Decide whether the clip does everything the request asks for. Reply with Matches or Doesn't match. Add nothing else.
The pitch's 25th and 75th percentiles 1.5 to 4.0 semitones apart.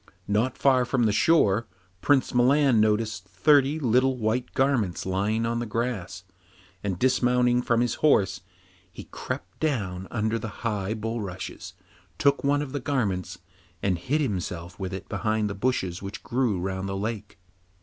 Doesn't match